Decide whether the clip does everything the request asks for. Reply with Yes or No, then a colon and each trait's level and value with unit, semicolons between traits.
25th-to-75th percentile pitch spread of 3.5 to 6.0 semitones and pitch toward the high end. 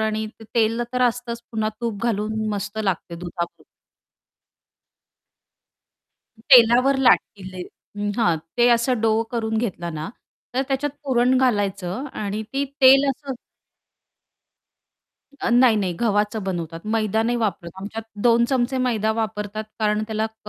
No: average, 2.9 semitones; high, 220 Hz